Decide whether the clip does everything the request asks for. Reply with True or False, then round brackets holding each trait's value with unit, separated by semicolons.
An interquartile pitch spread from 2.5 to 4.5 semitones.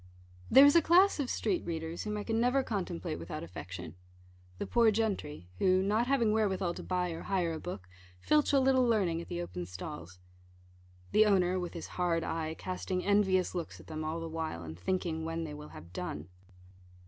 False (5.1 semitones)